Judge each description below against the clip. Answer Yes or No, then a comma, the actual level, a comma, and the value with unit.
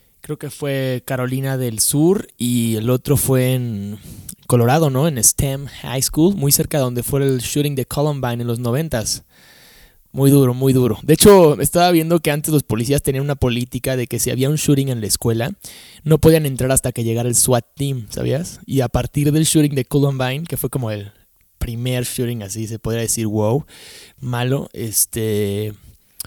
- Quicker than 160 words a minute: Yes, fast, 190 wpm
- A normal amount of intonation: Yes, average, 3.3 semitones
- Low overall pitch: Yes, low, 130 Hz